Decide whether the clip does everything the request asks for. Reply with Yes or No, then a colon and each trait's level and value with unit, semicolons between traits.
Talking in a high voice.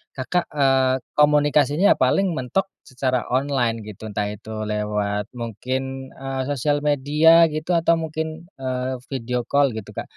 No: low, 135 Hz